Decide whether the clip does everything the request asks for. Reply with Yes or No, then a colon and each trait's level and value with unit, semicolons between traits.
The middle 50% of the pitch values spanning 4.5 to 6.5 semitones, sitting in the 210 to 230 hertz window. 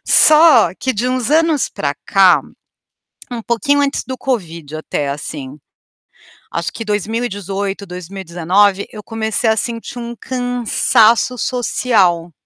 Yes: wide, 5.6 semitones; high, 215 Hz